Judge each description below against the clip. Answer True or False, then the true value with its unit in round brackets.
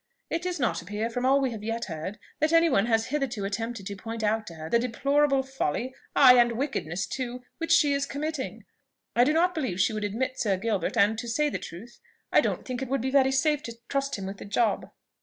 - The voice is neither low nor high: False (240 Hz)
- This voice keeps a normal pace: False (235 wpm)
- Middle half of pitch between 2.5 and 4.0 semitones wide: False (4.5 semitones)